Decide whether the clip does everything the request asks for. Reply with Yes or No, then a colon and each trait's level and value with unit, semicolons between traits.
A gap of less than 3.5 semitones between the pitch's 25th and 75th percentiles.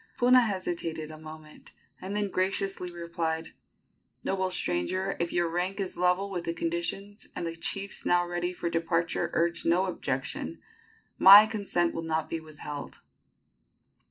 Yes: average, 2.7 semitones